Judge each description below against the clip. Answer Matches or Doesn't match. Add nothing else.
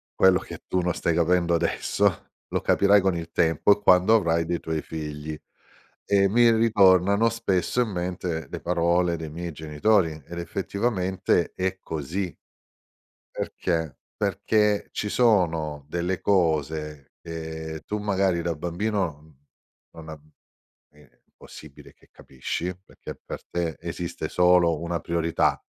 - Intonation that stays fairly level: Doesn't match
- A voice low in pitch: Matches